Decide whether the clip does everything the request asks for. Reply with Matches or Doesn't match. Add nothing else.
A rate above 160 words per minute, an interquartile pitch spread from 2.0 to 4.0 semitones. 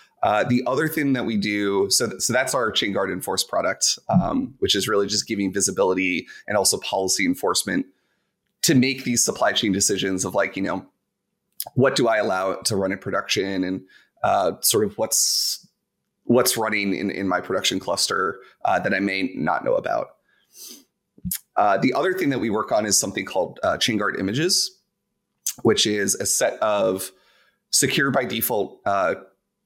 Doesn't match